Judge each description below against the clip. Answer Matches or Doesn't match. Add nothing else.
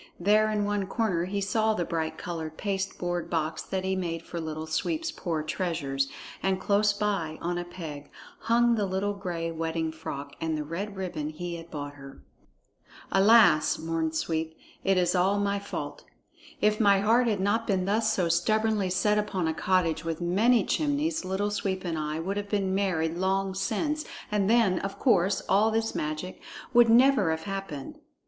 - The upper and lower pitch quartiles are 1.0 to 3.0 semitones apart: Doesn't match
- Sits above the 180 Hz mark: Matches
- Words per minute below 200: Matches